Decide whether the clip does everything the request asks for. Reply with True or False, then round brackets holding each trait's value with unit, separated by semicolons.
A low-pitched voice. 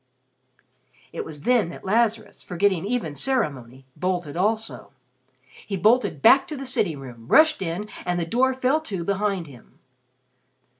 False (195 Hz)